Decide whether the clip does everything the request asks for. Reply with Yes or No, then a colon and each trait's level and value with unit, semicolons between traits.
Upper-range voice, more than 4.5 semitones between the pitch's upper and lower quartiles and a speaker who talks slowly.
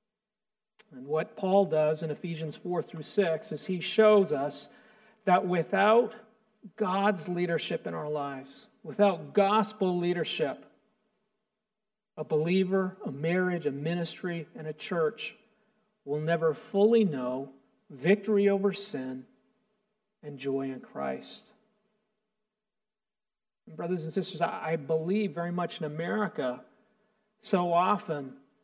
Yes: high, 195 Hz; average, 5.1 semitones; slow, 115 wpm